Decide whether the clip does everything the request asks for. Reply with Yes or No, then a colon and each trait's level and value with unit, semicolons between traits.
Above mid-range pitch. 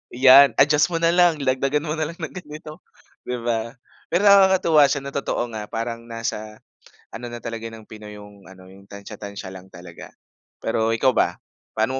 No: low, 120 Hz